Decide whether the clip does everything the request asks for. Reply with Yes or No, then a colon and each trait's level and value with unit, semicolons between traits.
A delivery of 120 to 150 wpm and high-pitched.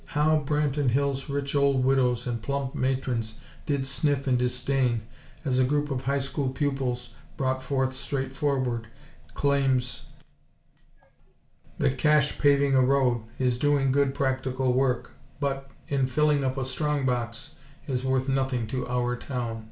No: average, 145 wpm; low, 135 Hz